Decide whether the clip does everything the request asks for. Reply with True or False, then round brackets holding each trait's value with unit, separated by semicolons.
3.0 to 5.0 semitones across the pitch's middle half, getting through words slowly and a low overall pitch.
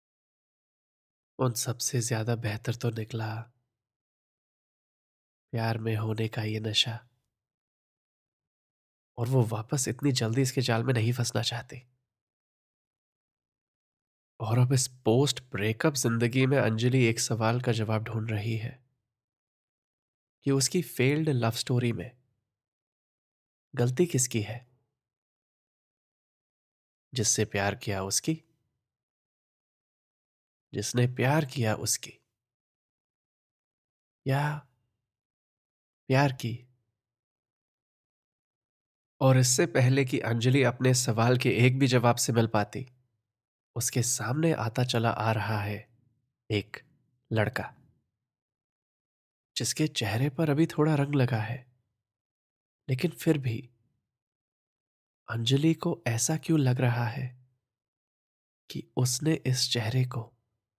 False (2.6 semitones; 105 wpm; 120 Hz)